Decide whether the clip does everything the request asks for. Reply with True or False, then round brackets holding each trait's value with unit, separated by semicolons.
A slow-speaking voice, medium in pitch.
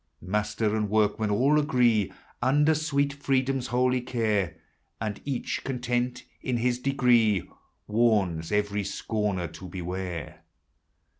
False (115 wpm; 115 Hz)